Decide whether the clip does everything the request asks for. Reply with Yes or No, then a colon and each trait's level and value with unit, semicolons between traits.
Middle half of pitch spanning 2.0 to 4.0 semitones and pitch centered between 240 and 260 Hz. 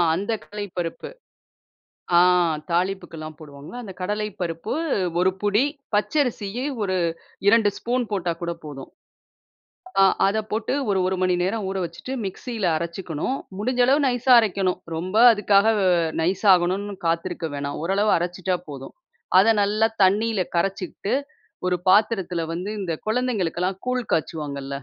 No: average, 3.7 semitones; high, 190 Hz